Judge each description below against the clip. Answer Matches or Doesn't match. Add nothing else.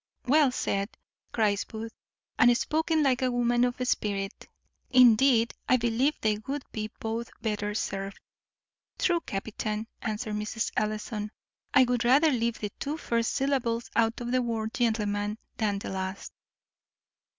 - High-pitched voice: Matches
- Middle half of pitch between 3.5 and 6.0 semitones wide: Doesn't match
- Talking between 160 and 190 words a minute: Doesn't match